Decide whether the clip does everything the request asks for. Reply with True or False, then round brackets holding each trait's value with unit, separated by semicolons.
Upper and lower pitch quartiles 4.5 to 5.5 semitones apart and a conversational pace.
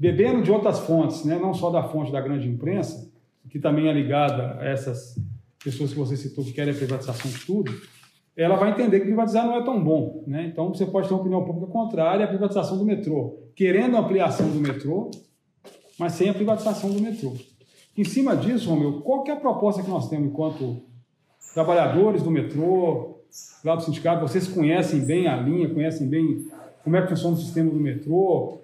False (4.8 semitones; 200 wpm)